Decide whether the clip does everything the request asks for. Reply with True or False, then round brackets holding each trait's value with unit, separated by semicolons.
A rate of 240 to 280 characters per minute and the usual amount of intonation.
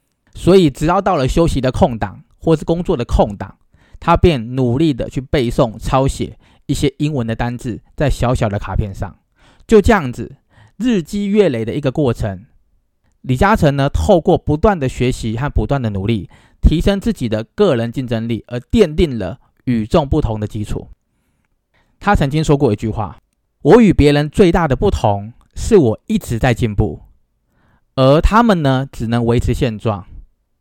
False (250 characters per minute; 6.4 semitones)